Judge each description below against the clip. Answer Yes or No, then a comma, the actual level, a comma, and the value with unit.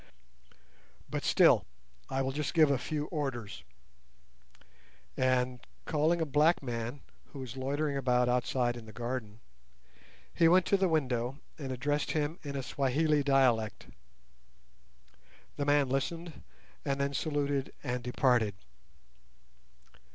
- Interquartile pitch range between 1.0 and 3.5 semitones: Yes, average, 3.0 semitones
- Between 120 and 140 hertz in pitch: Yes, low, 135 Hz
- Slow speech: Yes, slow, 125 wpm